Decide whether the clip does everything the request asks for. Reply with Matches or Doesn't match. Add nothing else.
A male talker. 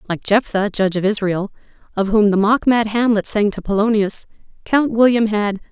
Doesn't match